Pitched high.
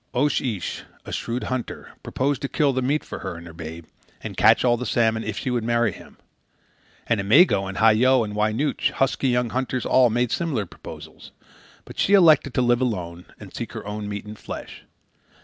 No: low, 120 Hz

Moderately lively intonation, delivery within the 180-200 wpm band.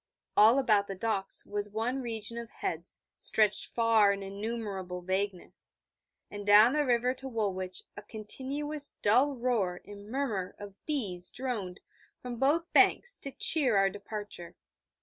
No: average, 4.1 semitones; average, 145 wpm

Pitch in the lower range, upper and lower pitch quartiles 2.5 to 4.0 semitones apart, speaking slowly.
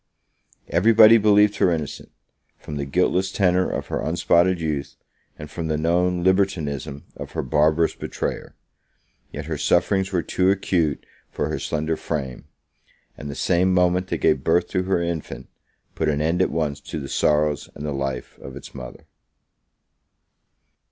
No: very low, 85 Hz; average, 3.6 semitones; average, 160 wpm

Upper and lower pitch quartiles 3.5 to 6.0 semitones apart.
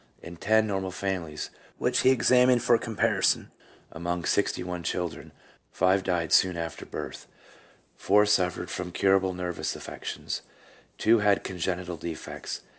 No: average, 2.9 semitones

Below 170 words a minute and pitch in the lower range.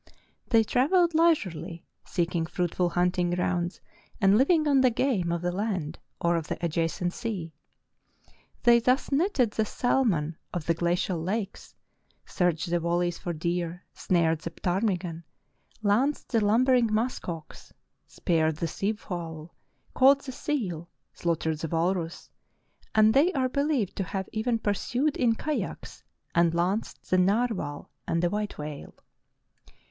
No: average, 140 wpm; medium, 185 Hz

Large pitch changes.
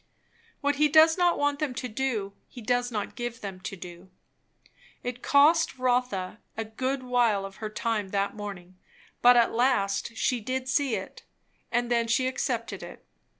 No: average, 4.0 semitones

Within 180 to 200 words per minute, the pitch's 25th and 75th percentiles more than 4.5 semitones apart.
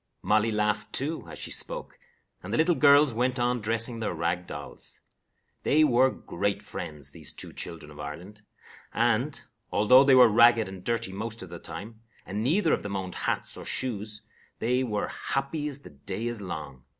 Yes: average, 185 wpm; average, 5.1 semitones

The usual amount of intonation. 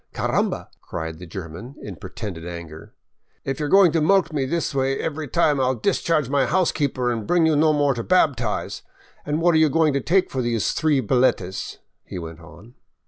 No: wide, 6.9 semitones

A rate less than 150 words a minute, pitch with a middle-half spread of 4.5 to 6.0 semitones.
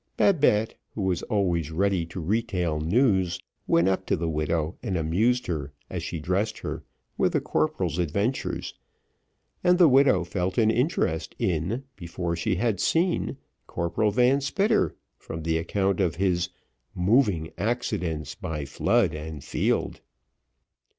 Yes: average, 140 wpm; average, 5.2 semitones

